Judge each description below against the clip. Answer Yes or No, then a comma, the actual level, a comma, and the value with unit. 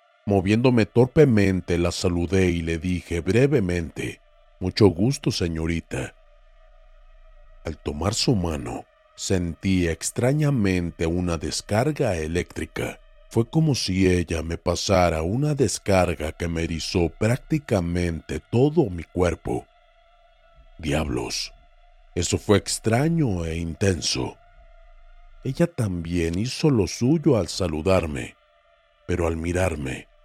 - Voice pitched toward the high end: No, low, 100 Hz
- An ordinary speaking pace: No, slow, 100 wpm